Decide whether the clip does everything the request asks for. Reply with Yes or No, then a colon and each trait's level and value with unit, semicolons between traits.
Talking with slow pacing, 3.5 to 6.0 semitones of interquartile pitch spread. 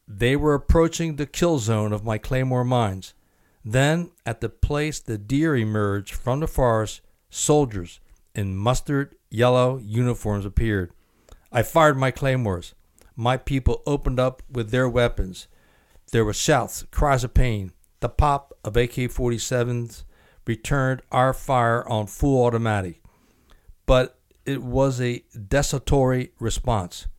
Yes: slow, 130 wpm; average, 4.0 semitones